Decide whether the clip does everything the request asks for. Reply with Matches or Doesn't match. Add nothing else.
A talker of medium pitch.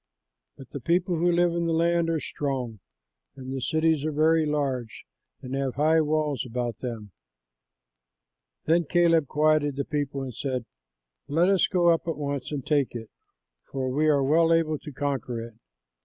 Matches